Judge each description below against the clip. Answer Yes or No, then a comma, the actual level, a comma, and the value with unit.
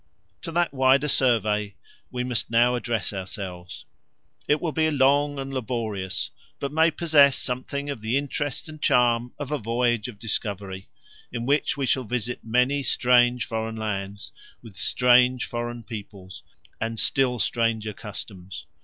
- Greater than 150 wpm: No, average, 145 wpm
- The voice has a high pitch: No, low, 120 Hz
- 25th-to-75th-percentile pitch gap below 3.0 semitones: No, average, 3.9 semitones